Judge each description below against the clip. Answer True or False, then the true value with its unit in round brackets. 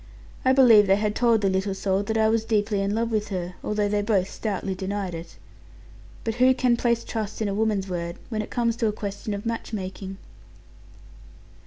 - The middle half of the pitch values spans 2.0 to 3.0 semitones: True (2.5 semitones)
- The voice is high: True (210 Hz)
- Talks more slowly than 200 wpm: False (205 wpm)